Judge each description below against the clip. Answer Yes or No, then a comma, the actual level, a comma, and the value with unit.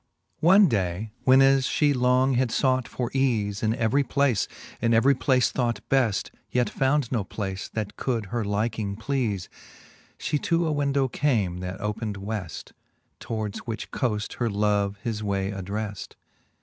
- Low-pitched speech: Yes, low, 115 Hz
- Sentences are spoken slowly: No, average, 160 wpm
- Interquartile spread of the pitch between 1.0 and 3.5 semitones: No, average, 4.4 semitones